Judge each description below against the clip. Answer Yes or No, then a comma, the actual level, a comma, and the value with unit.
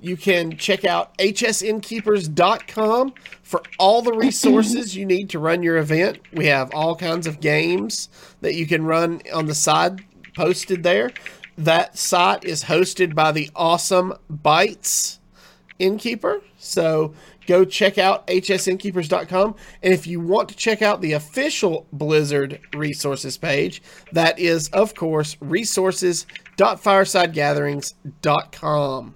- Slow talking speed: Yes, slow, 125 wpm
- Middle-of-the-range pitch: Yes, medium, 180 Hz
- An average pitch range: Yes, average, 3.9 semitones